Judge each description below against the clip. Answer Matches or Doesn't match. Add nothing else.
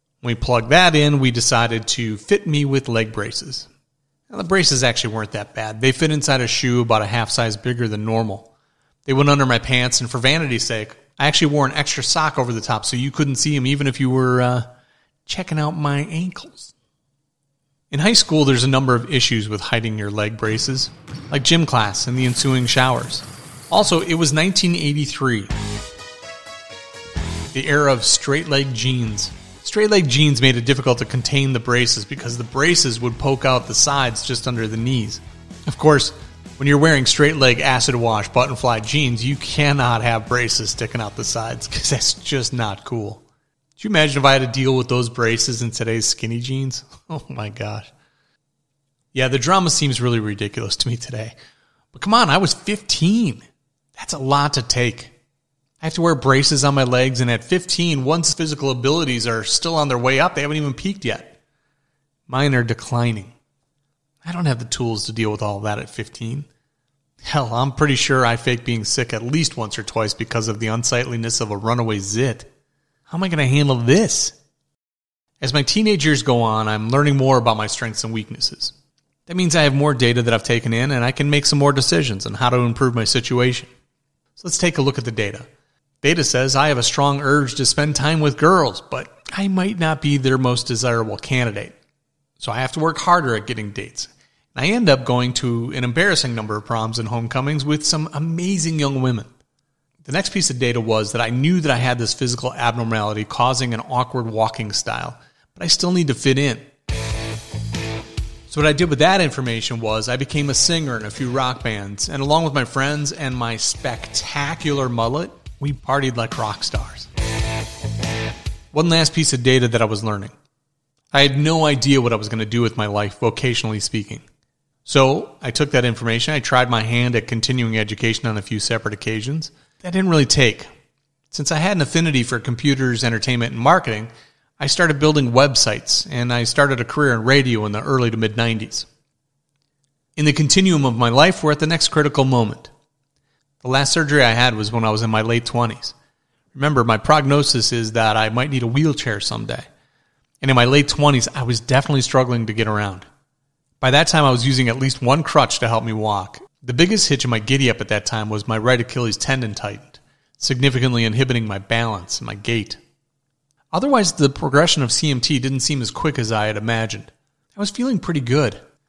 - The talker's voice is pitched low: Matches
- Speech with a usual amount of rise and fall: Matches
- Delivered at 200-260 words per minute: Matches